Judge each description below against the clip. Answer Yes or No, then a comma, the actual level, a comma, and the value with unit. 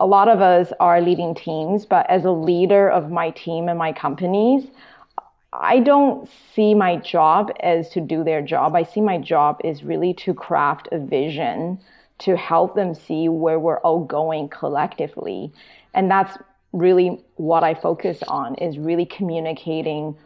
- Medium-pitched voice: Yes, medium, 175 Hz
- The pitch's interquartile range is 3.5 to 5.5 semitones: No, average, 3.1 semitones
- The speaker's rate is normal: Yes, average, 165 wpm